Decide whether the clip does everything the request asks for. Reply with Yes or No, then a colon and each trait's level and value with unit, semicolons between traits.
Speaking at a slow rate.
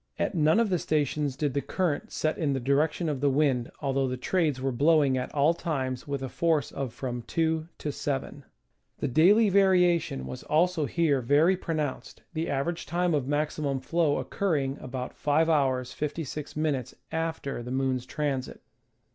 No: average, 165 wpm